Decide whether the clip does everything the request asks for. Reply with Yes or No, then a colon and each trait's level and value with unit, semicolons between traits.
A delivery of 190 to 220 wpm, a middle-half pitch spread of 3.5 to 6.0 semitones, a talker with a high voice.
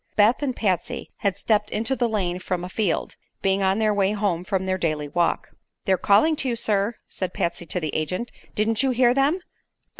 Yes: fast, 205 wpm; average, 3.8 semitones; high, 200 Hz